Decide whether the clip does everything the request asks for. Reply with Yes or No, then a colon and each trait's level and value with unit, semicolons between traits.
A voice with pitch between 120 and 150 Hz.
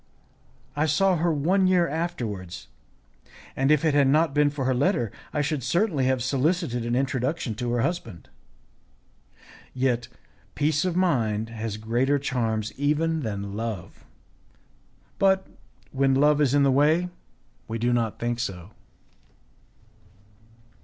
Yes: low, 135 Hz